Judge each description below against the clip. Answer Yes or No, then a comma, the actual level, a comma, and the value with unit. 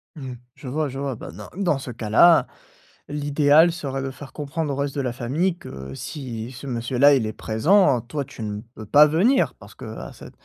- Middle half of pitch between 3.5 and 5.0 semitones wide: Yes, average, 4.1 semitones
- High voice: No, medium, 140 Hz